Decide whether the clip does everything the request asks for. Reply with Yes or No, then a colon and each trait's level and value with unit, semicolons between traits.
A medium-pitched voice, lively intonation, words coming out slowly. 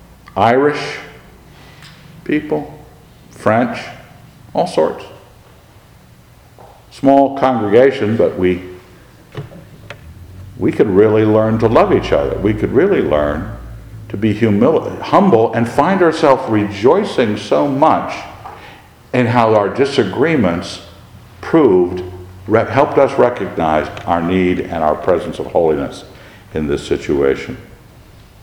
No: low, 110 Hz; wide, 5.7 semitones; slow, 105 wpm